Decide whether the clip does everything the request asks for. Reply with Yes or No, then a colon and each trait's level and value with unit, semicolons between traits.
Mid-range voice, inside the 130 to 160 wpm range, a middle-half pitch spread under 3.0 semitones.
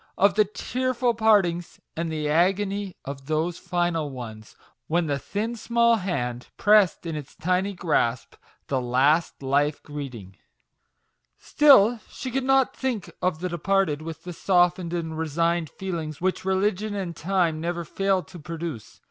No: medium, 175 Hz; average, 145 wpm; average, 4.2 semitones